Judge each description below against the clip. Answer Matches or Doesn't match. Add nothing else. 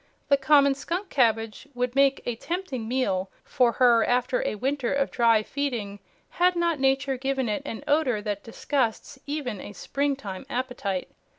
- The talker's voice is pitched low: Doesn't match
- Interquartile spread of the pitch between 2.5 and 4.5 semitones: Matches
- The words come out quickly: Doesn't match